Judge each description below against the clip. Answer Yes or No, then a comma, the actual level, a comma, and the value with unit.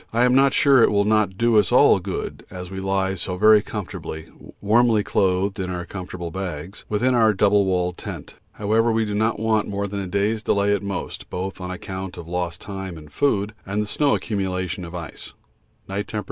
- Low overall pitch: Yes, low, 100 Hz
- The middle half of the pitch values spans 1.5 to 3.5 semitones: Yes, average, 2.7 semitones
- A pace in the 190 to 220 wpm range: Yes, fast, 205 wpm